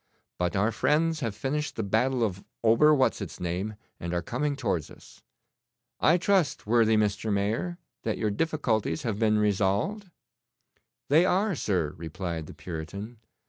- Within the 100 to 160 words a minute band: Yes, average, 150 wpm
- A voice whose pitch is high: No, low, 110 Hz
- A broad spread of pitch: Yes, wide, 7.0 semitones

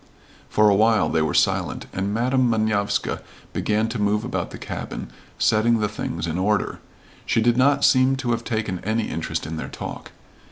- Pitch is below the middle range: Yes, low, 110 Hz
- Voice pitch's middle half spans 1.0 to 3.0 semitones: Yes, narrow, 2.6 semitones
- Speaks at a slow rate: No, average, 185 wpm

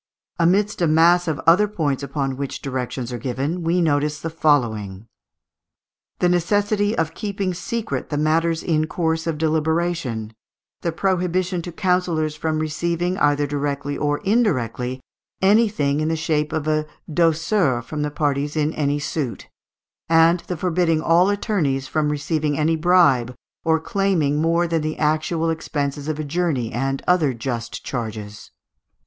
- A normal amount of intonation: Yes, average, 3.2 semitones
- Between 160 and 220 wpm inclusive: No, average, 150 wpm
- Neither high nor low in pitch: Yes, medium, 155 Hz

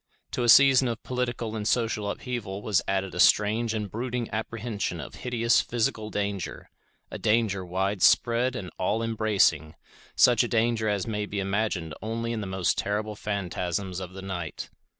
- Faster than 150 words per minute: Yes, average, 165 wpm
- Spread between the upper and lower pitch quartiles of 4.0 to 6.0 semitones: No, average, 3.2 semitones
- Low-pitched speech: Yes, low, 105 Hz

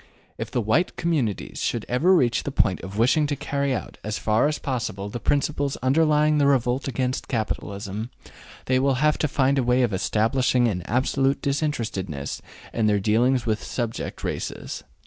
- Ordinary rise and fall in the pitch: Yes, average, 4.3 semitones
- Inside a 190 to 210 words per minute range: No, average, 170 wpm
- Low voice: Yes, low, 125 Hz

